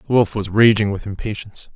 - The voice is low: Yes, low, 105 Hz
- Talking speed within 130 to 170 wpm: No, fast, 205 wpm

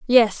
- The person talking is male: No, female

